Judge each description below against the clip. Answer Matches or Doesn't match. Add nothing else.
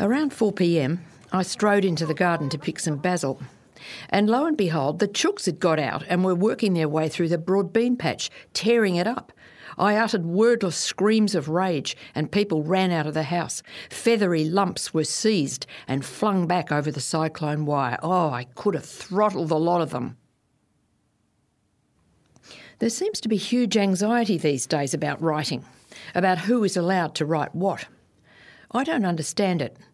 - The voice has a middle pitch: Matches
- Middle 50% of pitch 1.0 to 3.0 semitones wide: Doesn't match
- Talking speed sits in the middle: Matches